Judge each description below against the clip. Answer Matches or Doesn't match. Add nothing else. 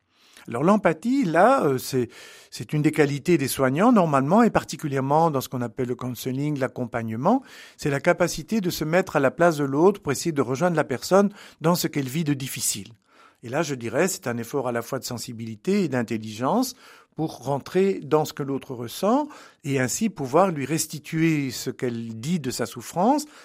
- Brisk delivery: Doesn't match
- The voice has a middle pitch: Matches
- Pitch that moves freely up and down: Matches